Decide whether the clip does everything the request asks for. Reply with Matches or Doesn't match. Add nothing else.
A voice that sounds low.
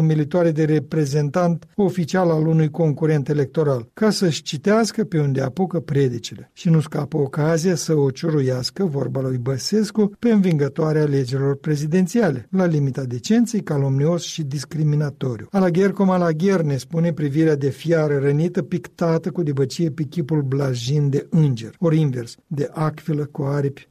Doesn't match